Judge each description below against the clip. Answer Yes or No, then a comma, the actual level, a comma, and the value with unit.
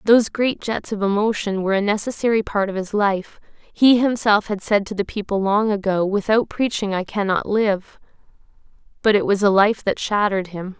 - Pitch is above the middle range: Yes, high, 205 Hz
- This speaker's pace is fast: No, average, 190 wpm